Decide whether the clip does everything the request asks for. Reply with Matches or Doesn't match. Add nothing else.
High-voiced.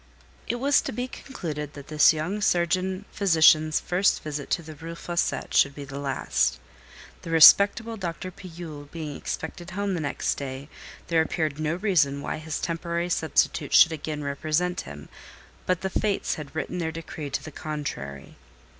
Doesn't match